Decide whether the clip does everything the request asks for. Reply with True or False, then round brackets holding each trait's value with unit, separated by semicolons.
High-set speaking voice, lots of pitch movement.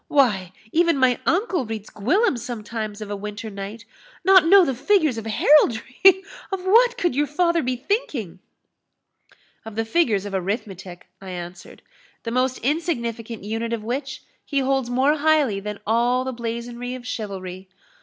True (240 Hz; 5.9 semitones)